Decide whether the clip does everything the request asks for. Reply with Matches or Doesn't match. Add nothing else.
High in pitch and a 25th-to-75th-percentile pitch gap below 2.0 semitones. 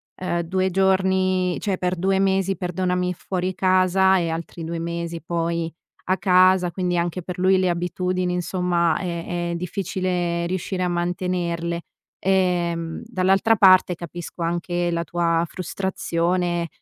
Doesn't match